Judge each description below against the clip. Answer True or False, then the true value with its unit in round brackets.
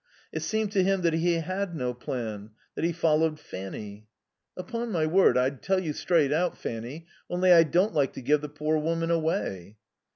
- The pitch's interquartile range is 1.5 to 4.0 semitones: False (4.9 semitones)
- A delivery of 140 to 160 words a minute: False (190 wpm)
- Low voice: False (160 Hz)